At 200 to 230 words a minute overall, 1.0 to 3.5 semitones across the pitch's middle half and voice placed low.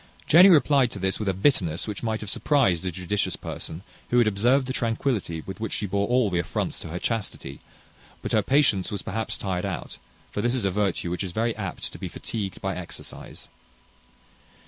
No: fast, 205 wpm; average, 4.3 semitones; low, 100 Hz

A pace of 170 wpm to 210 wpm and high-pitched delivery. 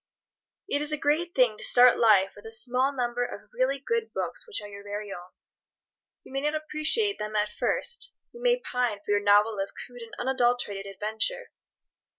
Yes: average, 190 wpm; high, 245 Hz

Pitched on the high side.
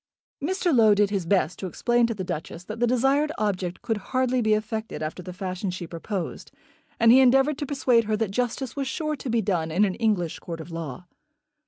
Yes: high, 215 Hz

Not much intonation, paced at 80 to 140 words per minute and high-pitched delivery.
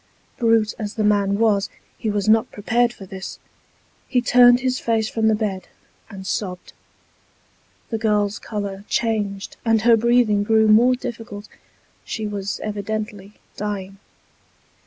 Yes: narrow, 1.9 semitones; slow, 135 wpm; high, 215 Hz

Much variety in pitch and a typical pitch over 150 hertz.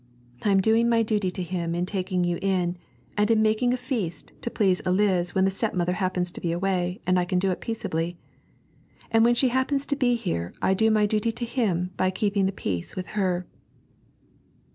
No: average, 3.6 semitones; high, 190 Hz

